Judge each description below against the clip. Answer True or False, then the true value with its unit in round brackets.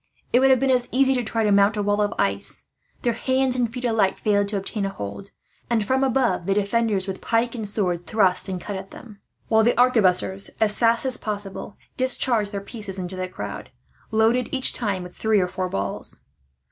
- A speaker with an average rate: False (210 wpm)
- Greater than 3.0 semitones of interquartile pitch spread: True (3.6 semitones)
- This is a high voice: True (210 Hz)